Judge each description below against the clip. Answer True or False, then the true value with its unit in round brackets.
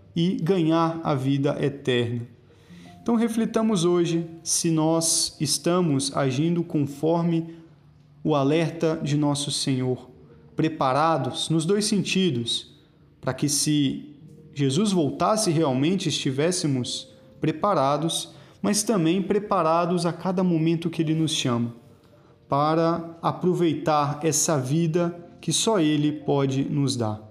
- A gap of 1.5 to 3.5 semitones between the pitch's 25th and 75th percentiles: True (3.0 semitones)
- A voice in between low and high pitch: True (160 Hz)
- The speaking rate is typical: False (110 wpm)